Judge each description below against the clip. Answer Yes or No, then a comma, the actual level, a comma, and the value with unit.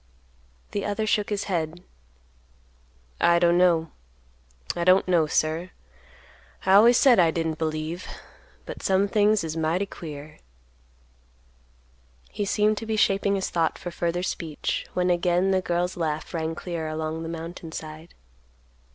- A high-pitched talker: No, medium, 170 Hz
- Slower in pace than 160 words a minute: Yes, average, 140 wpm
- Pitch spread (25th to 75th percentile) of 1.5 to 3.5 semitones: Yes, average, 3.1 semitones